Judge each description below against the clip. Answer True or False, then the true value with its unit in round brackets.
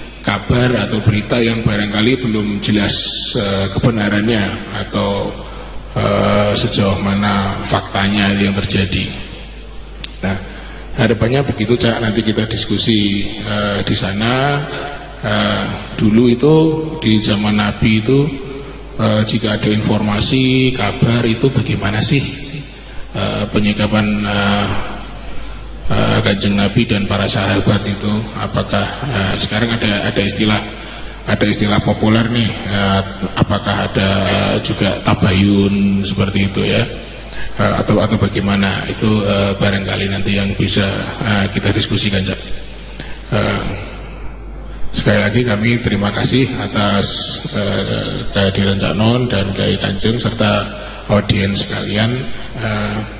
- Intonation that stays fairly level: True (2.2 semitones)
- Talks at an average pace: True (110 wpm)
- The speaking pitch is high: False (105 Hz)